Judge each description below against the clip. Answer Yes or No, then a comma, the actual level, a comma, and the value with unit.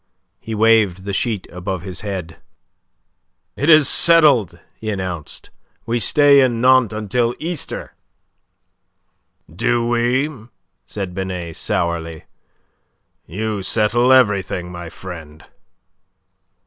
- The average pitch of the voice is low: Yes, low, 105 Hz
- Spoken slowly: Yes, slow, 100 wpm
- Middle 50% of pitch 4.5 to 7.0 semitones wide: Yes, average, 5.1 semitones